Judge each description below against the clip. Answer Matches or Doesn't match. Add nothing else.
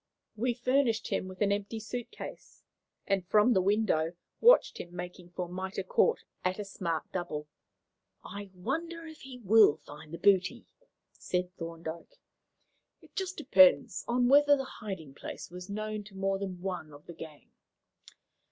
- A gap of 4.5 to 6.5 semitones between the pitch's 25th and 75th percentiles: Matches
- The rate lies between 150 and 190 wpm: Matches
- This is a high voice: Matches